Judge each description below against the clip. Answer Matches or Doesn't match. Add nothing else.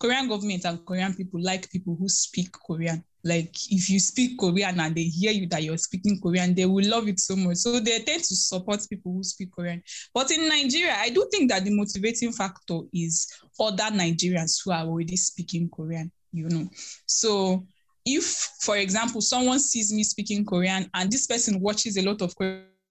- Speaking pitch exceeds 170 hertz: Matches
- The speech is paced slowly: Doesn't match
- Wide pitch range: Doesn't match